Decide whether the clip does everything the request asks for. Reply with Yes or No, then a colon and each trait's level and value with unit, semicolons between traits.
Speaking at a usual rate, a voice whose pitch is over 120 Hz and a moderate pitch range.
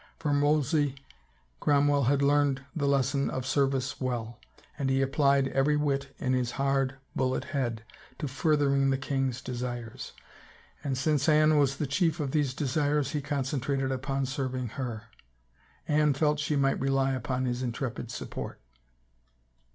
No: average, 145 wpm; low, 135 Hz; narrow, 1.9 semitones